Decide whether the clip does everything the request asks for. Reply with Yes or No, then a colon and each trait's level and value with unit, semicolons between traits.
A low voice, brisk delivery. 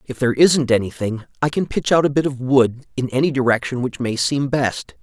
Yes: low, 130 Hz; fast, 225 wpm